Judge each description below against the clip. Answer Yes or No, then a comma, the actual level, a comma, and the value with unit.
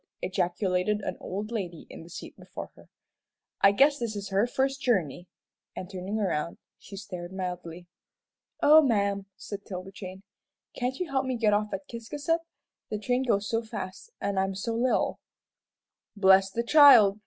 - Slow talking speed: No, average, 165 wpm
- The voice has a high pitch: Yes, high, 200 Hz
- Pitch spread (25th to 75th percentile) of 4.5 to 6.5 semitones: No, average, 3.9 semitones